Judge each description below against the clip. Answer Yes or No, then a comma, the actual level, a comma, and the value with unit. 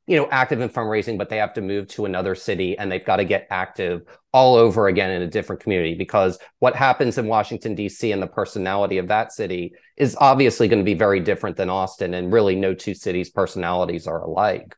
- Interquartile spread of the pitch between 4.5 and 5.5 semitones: No, average, 2.7 semitones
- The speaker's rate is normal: No, fast, 225 wpm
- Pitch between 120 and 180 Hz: No, very low, 95 Hz